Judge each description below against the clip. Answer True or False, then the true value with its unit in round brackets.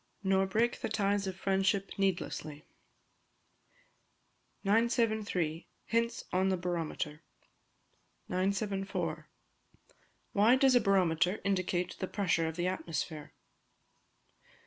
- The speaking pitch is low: False (190 Hz)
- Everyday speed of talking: False (95 wpm)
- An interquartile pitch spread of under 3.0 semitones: True (2.6 semitones)